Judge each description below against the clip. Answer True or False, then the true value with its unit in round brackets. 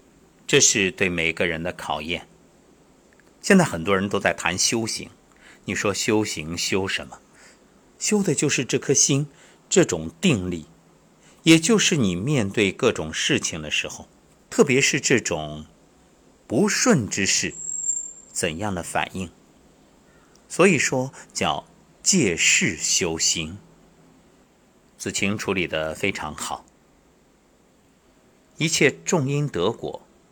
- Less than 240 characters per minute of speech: True (170 characters per minute)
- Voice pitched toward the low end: True (105 Hz)